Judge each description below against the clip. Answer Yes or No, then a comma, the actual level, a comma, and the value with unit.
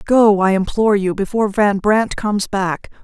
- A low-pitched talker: No, high, 205 Hz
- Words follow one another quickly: No, average, 180 wpm